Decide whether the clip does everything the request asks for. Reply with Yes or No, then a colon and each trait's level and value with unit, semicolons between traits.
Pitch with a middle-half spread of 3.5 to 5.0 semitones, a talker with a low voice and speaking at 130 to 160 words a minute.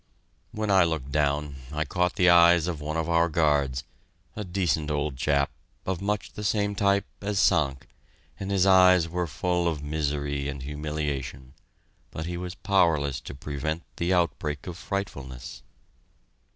Yes: average, 3.9 semitones; very low, 80 Hz; average, 155 wpm